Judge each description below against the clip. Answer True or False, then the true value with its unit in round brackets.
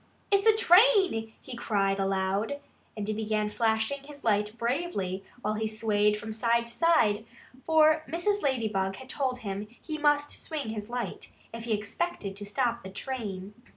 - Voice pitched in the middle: False (225 Hz)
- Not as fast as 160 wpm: False (170 wpm)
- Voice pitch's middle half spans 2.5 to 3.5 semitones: False (5.5 semitones)